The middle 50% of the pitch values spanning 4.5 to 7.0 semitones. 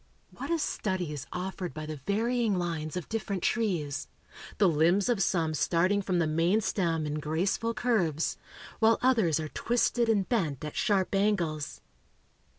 Yes: average, 5.3 semitones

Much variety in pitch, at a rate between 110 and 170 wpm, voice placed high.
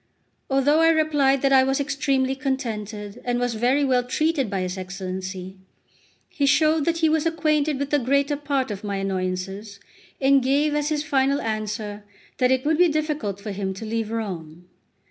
No: wide, 6.0 semitones; average, 180 wpm; very high, 260 Hz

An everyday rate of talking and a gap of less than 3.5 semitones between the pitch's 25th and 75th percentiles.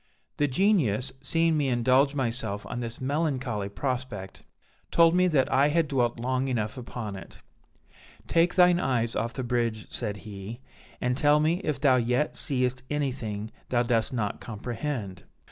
No: average, 155 wpm; average, 4.2 semitones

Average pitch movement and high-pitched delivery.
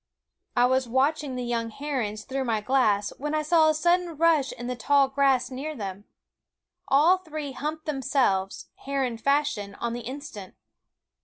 Yes: average, 4.1 semitones; very high, 270 Hz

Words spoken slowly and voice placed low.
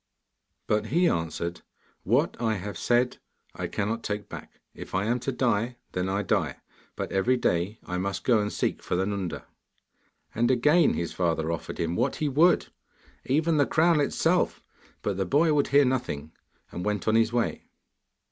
No: average, 175 wpm; low, 110 Hz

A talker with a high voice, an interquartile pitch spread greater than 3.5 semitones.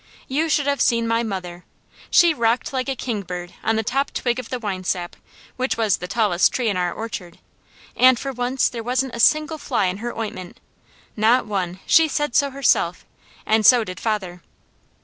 Yes: high, 230 Hz; average, 5.3 semitones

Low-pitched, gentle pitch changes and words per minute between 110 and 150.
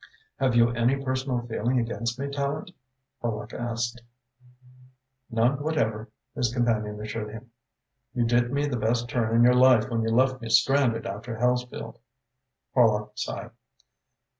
Yes: low, 120 Hz; narrow, 2.2 semitones; average, 140 wpm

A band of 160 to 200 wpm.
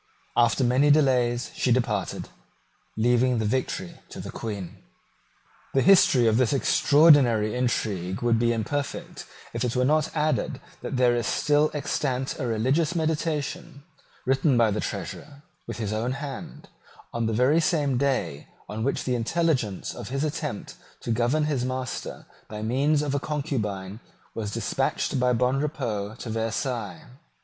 No: average, 150 wpm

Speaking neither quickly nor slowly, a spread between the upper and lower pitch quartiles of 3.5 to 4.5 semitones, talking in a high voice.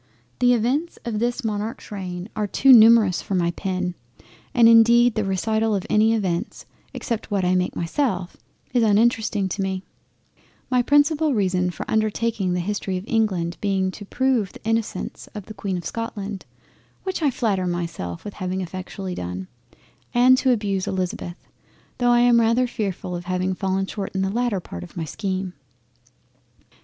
Yes: average, 170 wpm; average, 3.9 semitones; high, 205 Hz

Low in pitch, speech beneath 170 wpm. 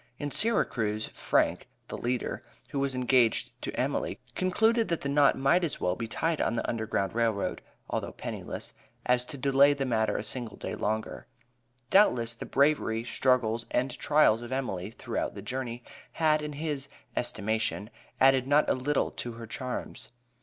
Yes: low, 125 Hz; average, 160 wpm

